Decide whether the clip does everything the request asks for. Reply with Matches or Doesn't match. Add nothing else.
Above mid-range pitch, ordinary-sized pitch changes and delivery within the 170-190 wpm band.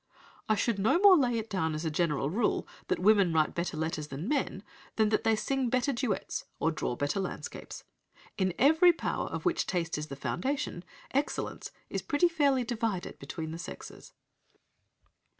Doesn't match